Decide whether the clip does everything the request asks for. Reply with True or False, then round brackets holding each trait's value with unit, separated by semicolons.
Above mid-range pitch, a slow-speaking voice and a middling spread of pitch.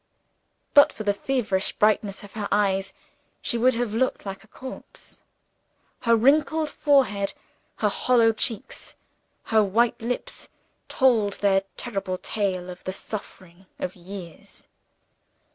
True (210 Hz; 125 wpm; 3.8 semitones)